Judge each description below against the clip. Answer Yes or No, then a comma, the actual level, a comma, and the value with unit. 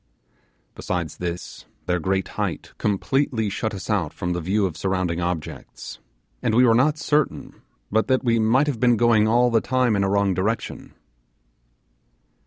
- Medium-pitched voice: No, low, 105 Hz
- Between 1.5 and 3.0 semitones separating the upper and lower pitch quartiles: No, average, 4.6 semitones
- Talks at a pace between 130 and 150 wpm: No, average, 165 wpm